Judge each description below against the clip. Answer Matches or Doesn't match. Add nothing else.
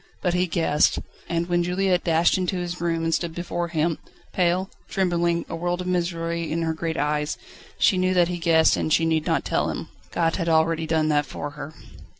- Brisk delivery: Matches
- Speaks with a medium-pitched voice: Matches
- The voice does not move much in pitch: Matches